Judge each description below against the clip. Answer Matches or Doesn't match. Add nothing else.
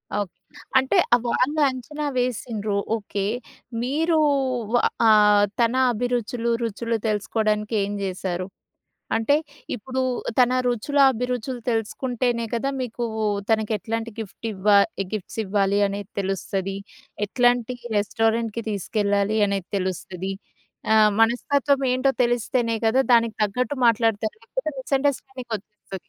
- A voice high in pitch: Matches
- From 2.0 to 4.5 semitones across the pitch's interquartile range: Matches